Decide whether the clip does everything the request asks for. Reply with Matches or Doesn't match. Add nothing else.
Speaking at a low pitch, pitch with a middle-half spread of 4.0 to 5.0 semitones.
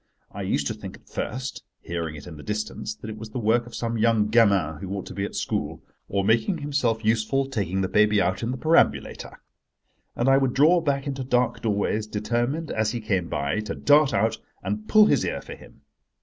Matches